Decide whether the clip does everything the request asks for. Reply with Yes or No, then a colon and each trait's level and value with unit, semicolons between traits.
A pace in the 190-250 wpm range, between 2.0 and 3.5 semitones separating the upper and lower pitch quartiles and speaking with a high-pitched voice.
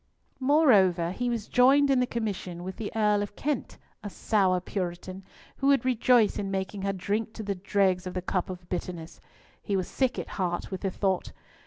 No: average, 195 wpm; average, 4.1 semitones; high, 200 Hz